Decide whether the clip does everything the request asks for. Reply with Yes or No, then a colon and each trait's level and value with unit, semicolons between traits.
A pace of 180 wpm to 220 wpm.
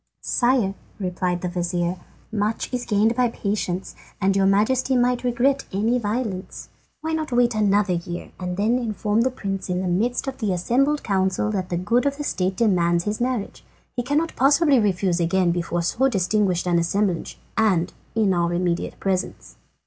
No: average, 170 wpm